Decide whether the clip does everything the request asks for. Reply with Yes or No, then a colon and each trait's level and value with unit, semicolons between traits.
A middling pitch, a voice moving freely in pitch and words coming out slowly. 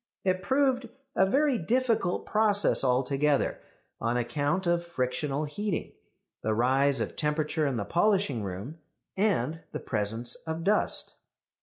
Yes: medium, 155 Hz; wide, 7.6 semitones; slow, 130 wpm